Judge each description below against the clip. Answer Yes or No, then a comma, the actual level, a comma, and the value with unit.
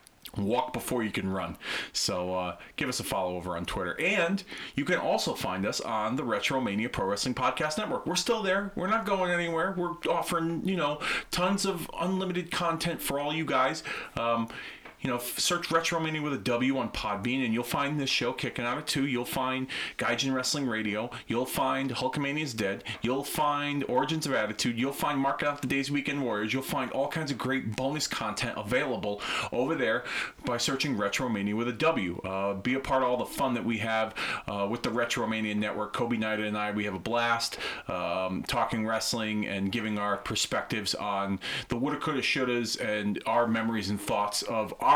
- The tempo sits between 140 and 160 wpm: No, fast, 205 wpm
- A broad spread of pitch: Yes, wide, 5.7 semitones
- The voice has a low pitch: Yes, low, 130 Hz